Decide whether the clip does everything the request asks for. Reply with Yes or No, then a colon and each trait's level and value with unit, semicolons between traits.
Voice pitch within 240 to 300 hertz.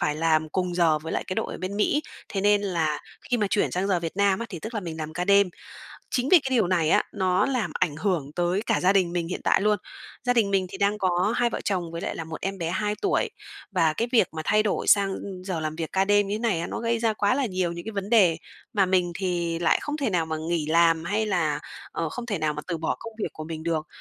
No: medium, 185 Hz